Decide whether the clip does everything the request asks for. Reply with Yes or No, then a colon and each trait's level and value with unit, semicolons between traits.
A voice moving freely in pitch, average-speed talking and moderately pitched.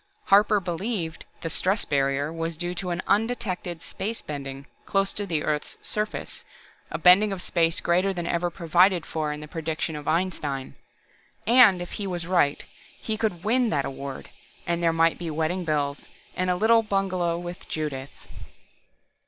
No: average, 3.8 semitones; average, 165 wpm; medium, 175 Hz